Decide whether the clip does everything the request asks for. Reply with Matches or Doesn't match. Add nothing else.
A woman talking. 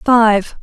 Matches